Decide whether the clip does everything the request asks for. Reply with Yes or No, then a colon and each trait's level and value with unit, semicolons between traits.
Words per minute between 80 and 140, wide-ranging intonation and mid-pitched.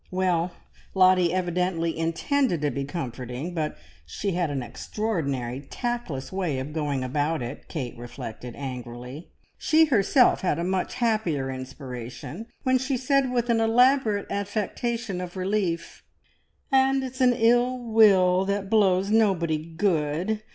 Yes: slow, 135 wpm; wide, 7.3 semitones; medium, 180 Hz